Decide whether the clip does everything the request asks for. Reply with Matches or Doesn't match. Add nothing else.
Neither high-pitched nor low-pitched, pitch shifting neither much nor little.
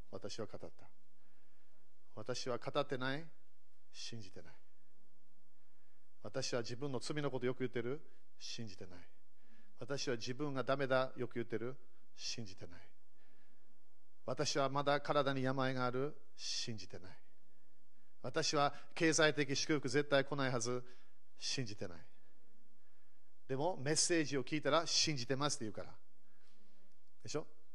Doesn't match